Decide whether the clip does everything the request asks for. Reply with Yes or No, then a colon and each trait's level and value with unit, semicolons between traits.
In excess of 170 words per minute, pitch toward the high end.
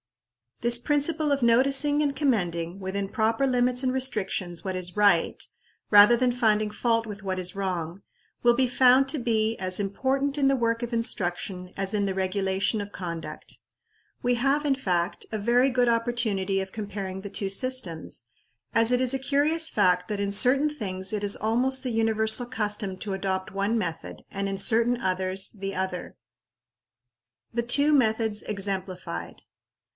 No: average, 165 wpm; high, 215 Hz